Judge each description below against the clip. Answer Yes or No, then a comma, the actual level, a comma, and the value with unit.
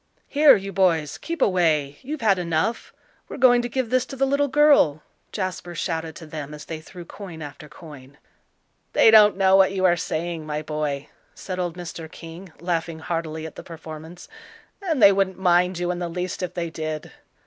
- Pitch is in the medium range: Yes, medium, 175 Hz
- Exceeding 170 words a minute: Yes, average, 190 wpm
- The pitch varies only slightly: No, average, 3.6 semitones